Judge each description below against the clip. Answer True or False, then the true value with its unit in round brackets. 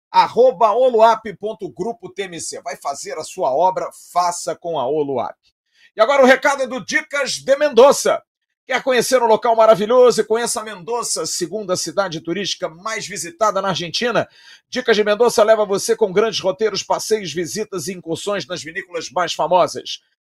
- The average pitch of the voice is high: True (215 Hz)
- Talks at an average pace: True (150 wpm)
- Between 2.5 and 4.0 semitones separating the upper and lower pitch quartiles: False (4.9 semitones)